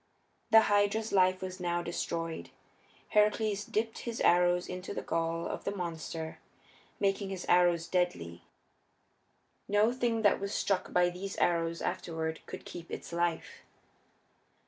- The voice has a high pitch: No, medium, 180 Hz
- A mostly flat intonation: No, average, 3.2 semitones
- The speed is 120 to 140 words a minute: Yes, slow, 135 wpm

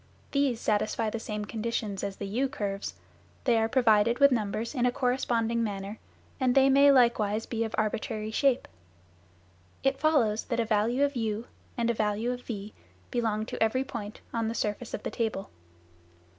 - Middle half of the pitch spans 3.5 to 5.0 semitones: No, average, 2.7 semitones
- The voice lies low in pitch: No, high, 230 Hz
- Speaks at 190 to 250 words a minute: No, average, 175 wpm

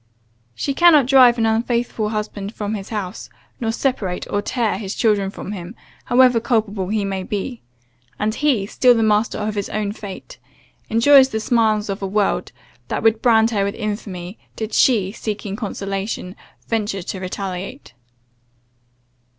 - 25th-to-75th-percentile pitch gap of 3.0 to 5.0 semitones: No, narrow, 2.6 semitones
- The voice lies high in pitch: Yes, high, 215 Hz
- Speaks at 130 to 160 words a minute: Yes, average, 155 wpm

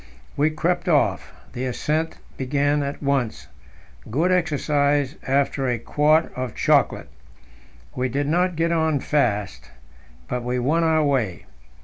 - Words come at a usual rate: No, slow, 130 wpm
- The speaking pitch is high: No, medium, 145 Hz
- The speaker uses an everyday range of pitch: Yes, average, 3.5 semitones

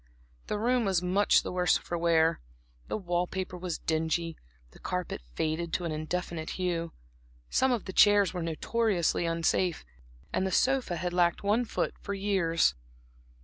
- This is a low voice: No, medium, 180 Hz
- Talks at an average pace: Yes, average, 160 wpm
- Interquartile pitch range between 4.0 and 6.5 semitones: No, average, 3.0 semitones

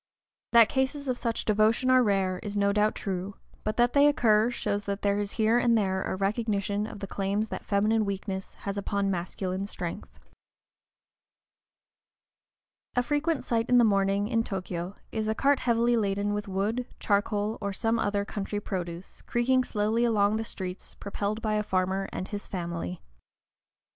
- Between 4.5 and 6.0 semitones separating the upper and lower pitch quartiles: No, narrow, 2.6 semitones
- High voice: Yes, high, 205 Hz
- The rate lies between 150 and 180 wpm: Yes, average, 170 wpm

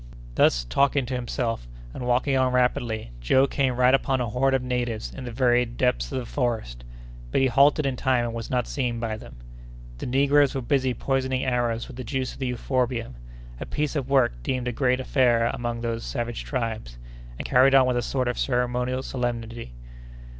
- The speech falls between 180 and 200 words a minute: Yes, average, 195 wpm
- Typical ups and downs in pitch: No, narrow, 2.1 semitones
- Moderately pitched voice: No, low, 125 Hz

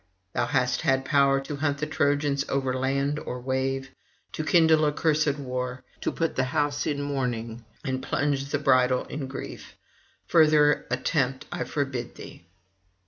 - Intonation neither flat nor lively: No, narrow, 2.2 semitones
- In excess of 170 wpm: No, average, 150 wpm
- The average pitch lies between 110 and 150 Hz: Yes, medium, 140 Hz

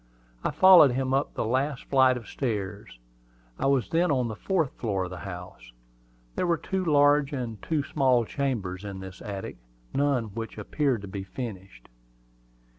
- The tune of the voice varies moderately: No, wide, 6.1 semitones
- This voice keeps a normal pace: Yes, average, 175 wpm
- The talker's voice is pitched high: No, low, 125 Hz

